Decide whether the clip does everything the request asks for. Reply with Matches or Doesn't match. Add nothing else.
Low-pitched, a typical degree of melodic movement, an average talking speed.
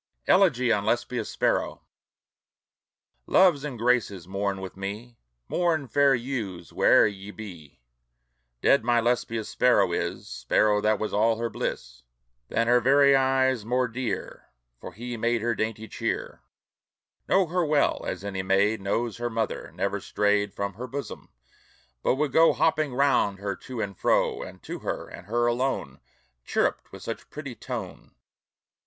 Matches